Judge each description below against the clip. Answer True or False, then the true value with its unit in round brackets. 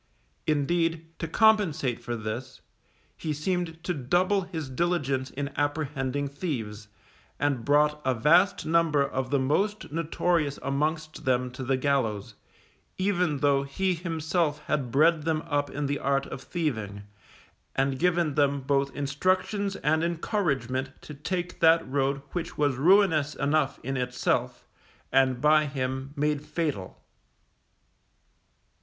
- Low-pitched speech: False (145 Hz)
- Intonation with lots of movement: False (3.7 semitones)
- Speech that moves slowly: True (130 wpm)